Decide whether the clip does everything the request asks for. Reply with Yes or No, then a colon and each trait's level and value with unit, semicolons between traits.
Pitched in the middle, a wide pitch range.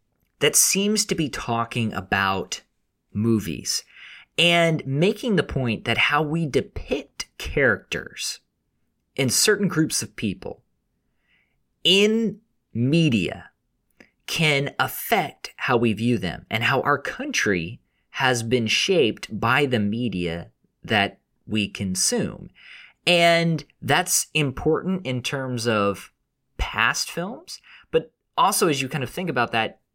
No: low, 130 Hz; wide, 6.4 semitones